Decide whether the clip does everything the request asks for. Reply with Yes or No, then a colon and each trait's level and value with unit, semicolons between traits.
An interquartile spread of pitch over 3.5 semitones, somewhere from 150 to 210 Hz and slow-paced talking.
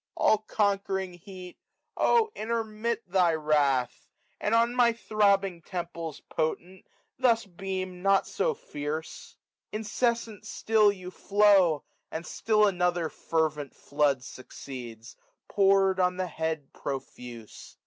Yes: average, 4.8 semitones; medium, 185 Hz; slow, 120 wpm